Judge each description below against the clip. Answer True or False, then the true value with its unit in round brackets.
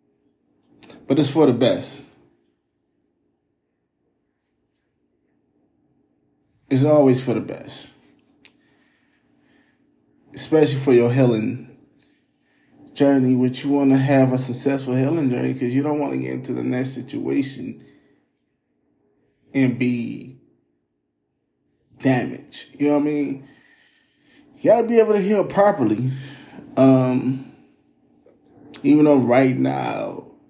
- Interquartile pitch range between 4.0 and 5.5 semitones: False (2.9 semitones)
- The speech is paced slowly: True (110 wpm)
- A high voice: False (135 Hz)